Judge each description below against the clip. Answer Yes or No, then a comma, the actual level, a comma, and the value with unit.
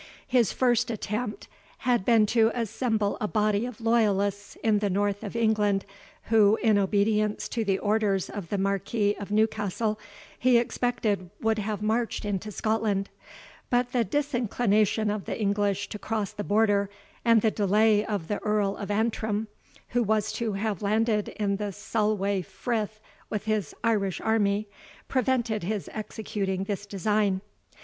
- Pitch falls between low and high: No, high, 210 Hz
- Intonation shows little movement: Yes, narrow, 1.7 semitones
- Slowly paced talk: No, average, 150 wpm